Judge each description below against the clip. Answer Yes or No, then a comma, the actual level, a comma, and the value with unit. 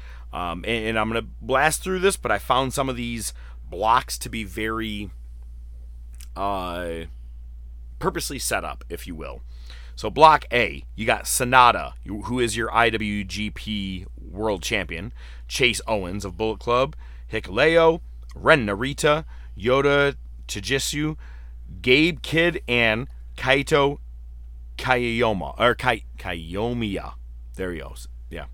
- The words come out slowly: Yes, slow, 125 wpm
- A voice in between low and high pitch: No, very low, 95 Hz